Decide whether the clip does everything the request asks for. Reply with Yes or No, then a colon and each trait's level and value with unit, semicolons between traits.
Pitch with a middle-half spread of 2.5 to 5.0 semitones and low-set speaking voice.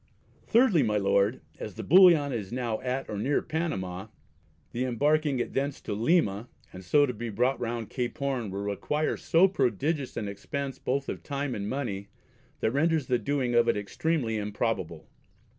No: wide, 5.4 semitones; low, 125 Hz